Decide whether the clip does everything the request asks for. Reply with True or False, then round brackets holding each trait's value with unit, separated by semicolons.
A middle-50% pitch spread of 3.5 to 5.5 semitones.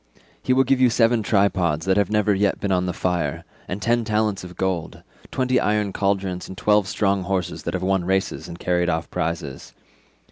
False (2.9 semitones)